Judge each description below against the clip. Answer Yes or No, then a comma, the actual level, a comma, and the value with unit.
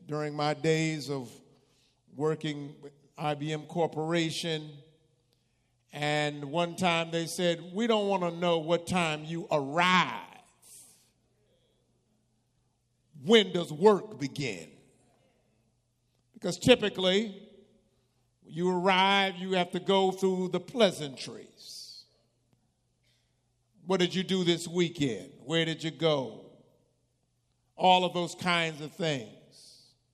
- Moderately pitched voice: Yes, medium, 155 Hz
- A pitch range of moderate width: No, wide, 5.7 semitones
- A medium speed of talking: No, slow, 105 wpm